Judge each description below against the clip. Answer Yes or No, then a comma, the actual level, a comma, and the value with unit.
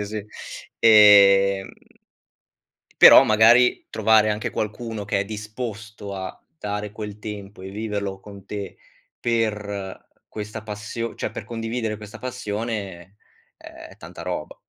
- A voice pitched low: Yes, low, 105 Hz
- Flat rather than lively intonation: Yes, narrow, 1.8 semitones